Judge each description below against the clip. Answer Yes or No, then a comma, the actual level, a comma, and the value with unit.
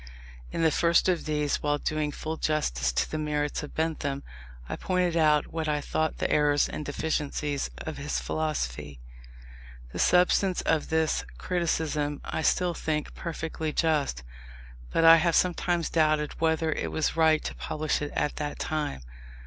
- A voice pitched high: No, medium, 155 Hz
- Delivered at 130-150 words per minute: No, average, 160 wpm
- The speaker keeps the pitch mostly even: Yes, narrow, 1.7 semitones